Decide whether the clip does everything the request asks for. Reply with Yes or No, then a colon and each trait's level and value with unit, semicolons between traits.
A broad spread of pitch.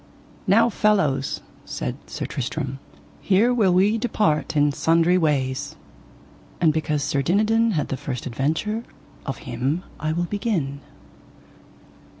Yes: wide, 6.6 semitones